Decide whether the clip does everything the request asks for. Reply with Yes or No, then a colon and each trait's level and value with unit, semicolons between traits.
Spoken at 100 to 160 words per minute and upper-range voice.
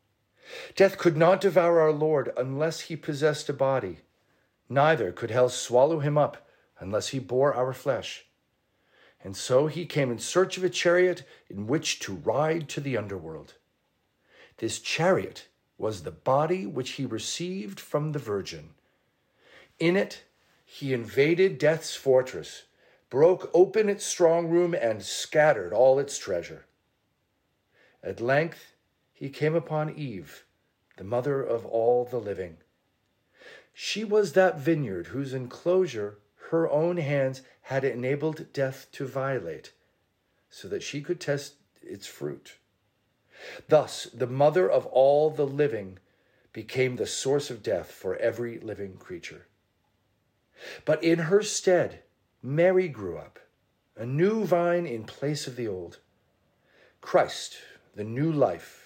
No: slow, 135 wpm; medium, 145 Hz